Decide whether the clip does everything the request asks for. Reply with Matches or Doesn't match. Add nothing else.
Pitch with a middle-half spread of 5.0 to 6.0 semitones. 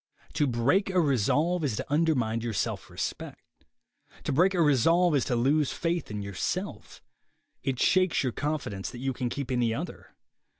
Matches